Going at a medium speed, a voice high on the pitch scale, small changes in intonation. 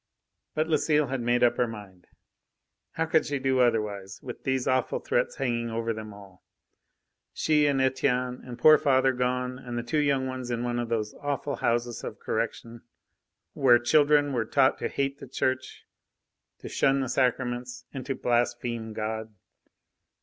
No: average, 165 wpm; low, 125 Hz; narrow, 2.3 semitones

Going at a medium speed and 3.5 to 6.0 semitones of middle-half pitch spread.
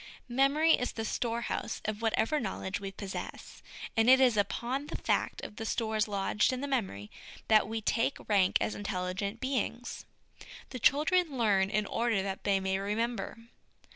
Yes: average, 170 wpm; average, 3.9 semitones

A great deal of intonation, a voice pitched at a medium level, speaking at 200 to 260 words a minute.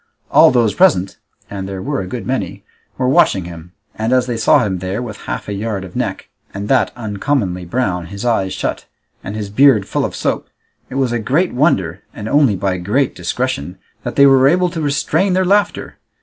No: wide, 6.0 semitones; low, 110 Hz; fast, 205 wpm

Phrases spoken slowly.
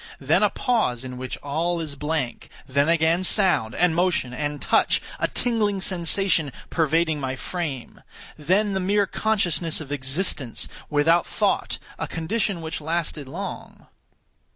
Yes: slow, 130 wpm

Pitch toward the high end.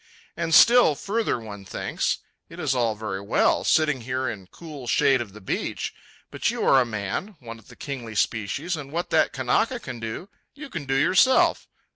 No: low, 130 Hz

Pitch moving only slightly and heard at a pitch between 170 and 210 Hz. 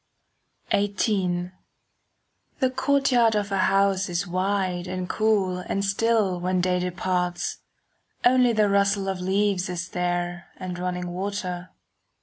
Yes: narrow, 2.2 semitones; high, 190 Hz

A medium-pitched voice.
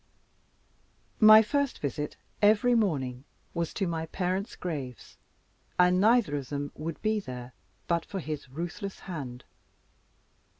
Yes: medium, 170 Hz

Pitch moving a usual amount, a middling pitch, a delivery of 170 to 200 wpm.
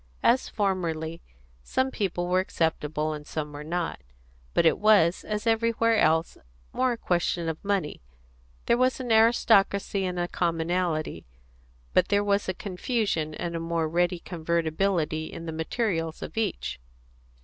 No: average, 4.2 semitones; medium, 175 Hz; average, 150 wpm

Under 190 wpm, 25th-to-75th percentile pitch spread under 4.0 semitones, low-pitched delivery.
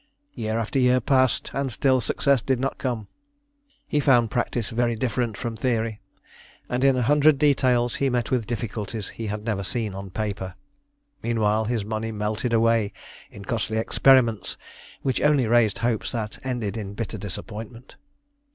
Yes: average, 160 wpm; average, 2.8 semitones; low, 115 Hz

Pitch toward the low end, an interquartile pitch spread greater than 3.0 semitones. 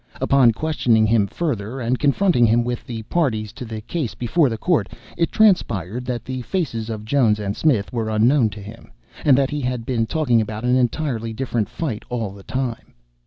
Yes: low, 120 Hz; average, 3.7 semitones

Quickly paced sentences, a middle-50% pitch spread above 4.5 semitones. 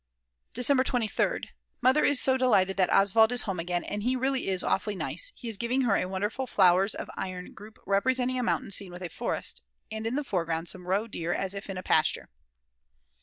Yes: fast, 210 wpm; average, 5.1 semitones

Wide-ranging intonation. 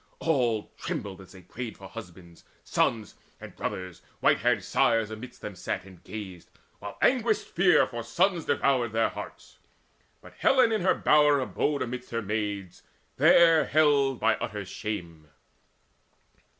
Yes: wide, 6.8 semitones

